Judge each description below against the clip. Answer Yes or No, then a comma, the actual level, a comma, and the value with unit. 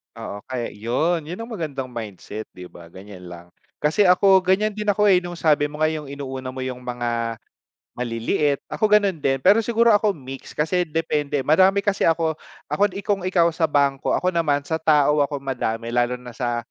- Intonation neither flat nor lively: No, wide, 6.6 semitones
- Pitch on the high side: No, medium, 150 Hz